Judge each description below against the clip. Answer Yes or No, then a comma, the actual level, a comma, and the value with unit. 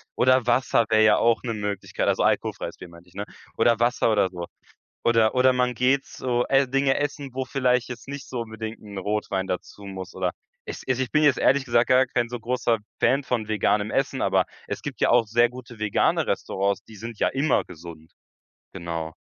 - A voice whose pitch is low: Yes, low, 115 Hz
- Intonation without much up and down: No, average, 3.7 semitones